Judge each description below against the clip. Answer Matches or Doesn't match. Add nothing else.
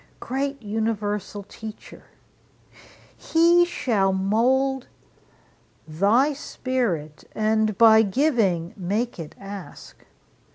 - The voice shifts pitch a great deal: Doesn't match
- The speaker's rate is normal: Doesn't match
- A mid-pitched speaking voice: Doesn't match